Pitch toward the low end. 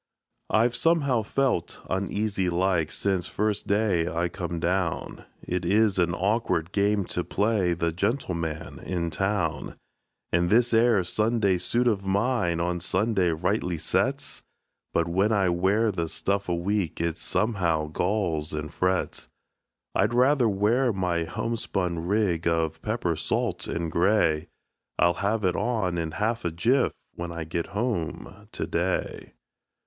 Yes: very low, 95 Hz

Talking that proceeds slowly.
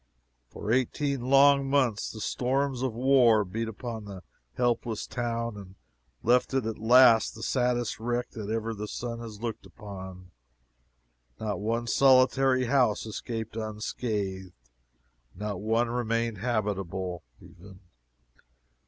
Yes: slow, 125 wpm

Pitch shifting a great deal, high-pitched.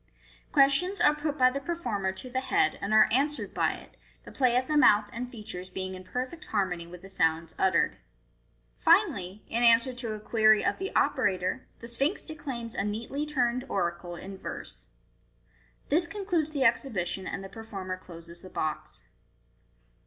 Yes: wide, 6.5 semitones; high, 230 Hz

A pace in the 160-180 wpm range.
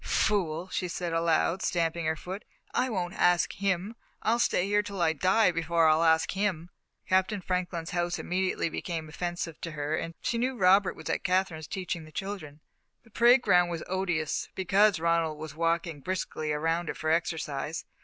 Yes: average, 175 wpm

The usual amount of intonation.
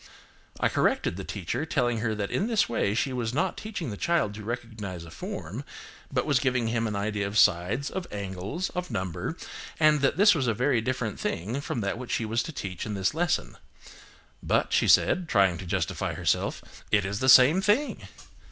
No: wide, 6.4 semitones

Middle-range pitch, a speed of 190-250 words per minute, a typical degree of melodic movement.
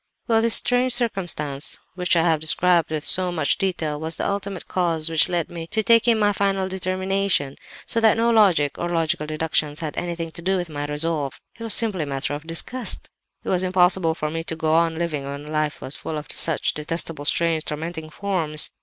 Yes: medium, 165 Hz; average, 195 wpm; average, 3.7 semitones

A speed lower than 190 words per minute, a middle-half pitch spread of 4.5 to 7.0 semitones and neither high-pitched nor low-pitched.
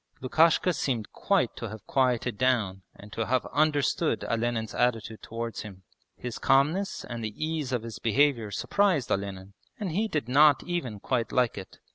No: average, 165 wpm; average, 4.9 semitones; low, 125 Hz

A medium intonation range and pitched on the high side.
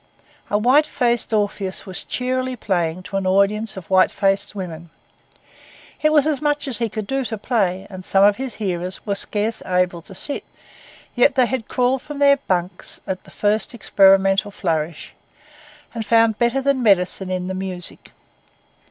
Yes: average, 4.7 semitones; high, 205 Hz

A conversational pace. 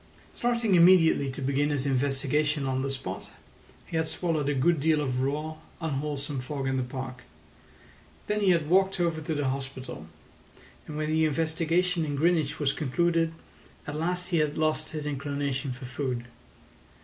Yes: average, 165 wpm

